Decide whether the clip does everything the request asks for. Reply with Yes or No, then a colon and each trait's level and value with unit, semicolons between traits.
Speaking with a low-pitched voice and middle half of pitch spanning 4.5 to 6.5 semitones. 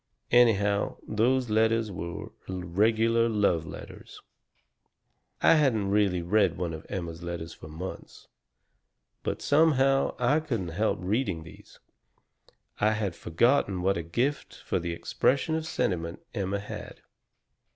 Yes: low, 100 Hz; average, 5.3 semitones